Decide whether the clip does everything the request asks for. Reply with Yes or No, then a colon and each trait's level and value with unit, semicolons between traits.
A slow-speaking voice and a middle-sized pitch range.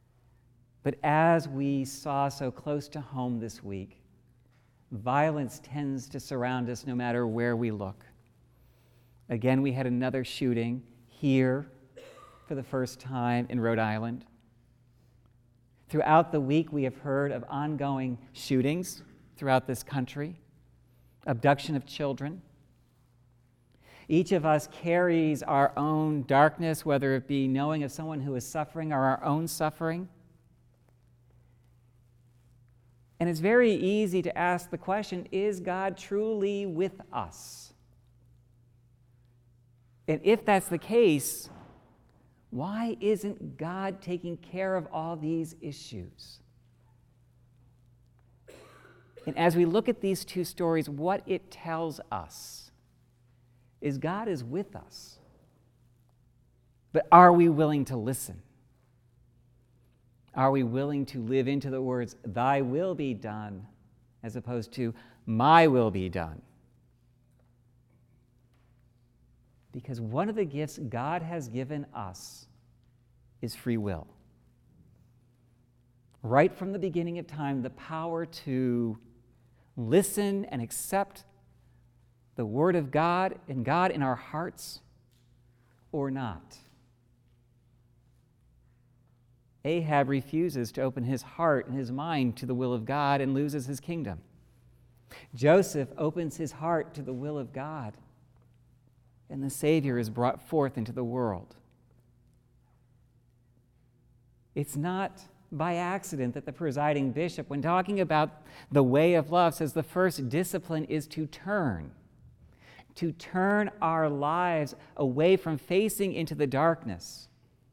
Yes: slow, 120 wpm; average, 4.4 semitones